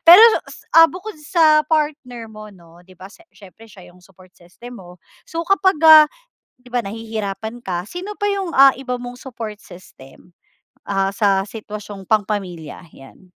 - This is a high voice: Yes, high, 220 Hz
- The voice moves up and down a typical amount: No, wide, 7.8 semitones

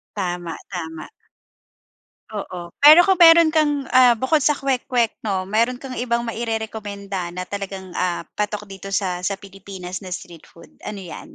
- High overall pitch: Yes, high, 205 Hz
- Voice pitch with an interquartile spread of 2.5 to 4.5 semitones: No, average, 5.1 semitones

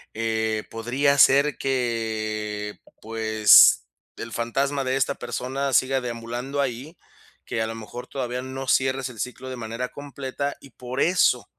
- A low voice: Yes, low, 125 Hz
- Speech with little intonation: No, average, 3.0 semitones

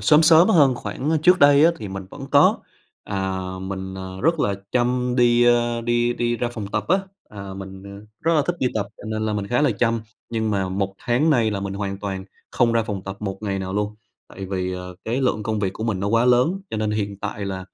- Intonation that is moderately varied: Yes, average, 4.0 semitones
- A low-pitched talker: Yes, low, 110 Hz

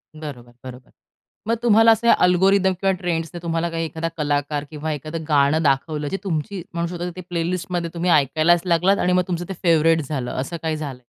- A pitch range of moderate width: Yes, average, 3.1 semitones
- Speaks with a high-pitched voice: No, medium, 165 Hz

